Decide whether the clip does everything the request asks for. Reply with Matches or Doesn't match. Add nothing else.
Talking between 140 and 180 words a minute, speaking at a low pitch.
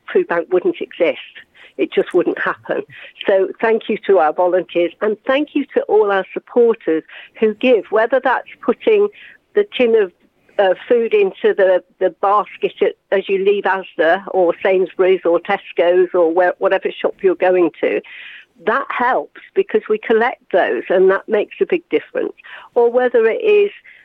Doesn't match